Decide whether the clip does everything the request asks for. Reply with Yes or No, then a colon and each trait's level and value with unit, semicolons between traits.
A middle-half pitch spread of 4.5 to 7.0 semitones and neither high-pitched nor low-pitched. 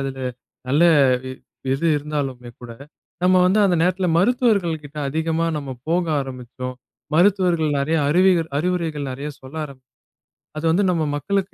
Yes: average, 4.8 semitones; medium, 160 Hz